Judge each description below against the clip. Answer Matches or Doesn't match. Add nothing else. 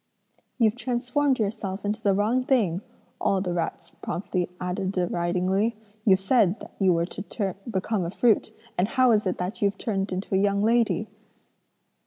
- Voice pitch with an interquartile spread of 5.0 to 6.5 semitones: Doesn't match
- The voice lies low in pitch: Doesn't match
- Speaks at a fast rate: Doesn't match